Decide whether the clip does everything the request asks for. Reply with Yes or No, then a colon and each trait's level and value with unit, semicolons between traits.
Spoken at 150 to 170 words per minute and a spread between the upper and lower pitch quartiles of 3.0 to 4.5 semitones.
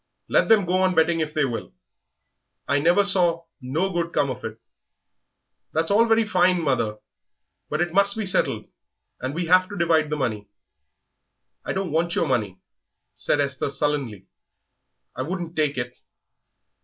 No: average, 160 wpm; average, 5.3 semitones